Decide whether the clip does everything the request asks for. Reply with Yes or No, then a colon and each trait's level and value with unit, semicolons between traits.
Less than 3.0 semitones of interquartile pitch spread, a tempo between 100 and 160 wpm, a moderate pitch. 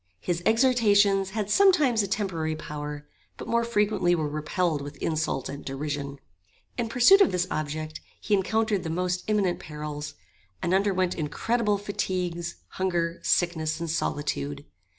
No: average, 5.2 semitones; average, 140 wpm; medium, 175 Hz